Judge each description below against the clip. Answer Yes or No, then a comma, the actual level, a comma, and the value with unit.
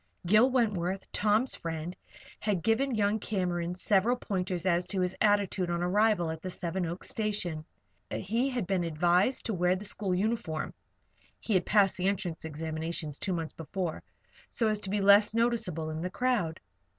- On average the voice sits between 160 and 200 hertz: Yes, high, 190 Hz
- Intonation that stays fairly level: No, average, 3.7 semitones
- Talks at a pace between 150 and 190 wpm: Yes, average, 170 wpm